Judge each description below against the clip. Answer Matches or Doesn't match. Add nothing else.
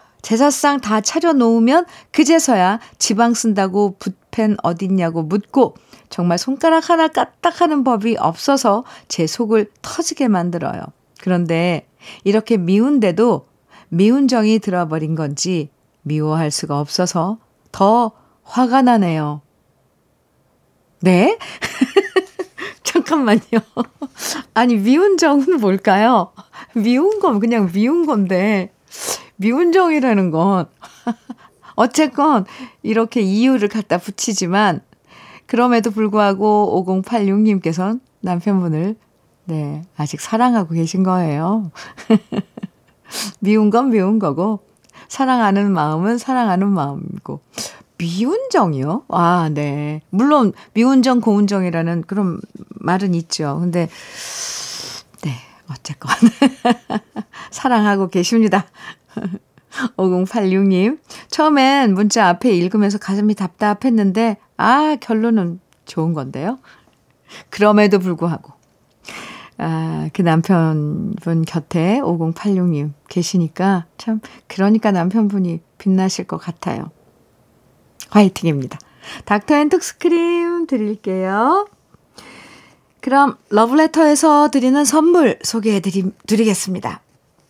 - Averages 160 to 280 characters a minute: Matches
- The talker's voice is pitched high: Matches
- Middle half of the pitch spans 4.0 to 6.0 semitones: Matches